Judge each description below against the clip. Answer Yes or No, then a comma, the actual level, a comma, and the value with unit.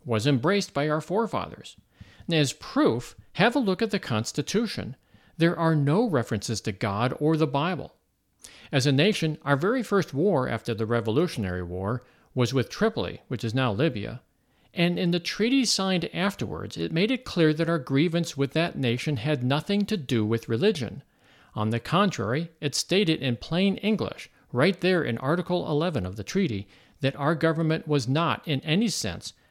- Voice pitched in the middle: Yes, medium, 150 Hz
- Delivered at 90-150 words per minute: No, average, 175 wpm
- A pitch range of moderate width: No, wide, 6.9 semitones